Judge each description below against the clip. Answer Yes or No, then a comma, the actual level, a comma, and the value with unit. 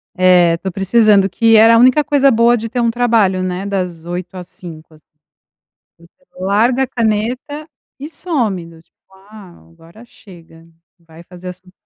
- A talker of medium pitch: No, high, 195 Hz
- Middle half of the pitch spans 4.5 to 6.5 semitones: Yes, average, 4.8 semitones